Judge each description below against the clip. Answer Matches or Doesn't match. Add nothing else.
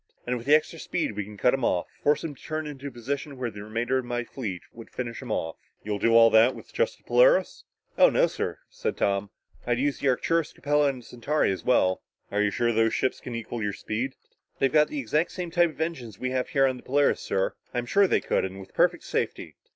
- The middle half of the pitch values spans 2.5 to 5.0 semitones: Matches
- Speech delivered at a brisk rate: Matches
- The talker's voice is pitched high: Doesn't match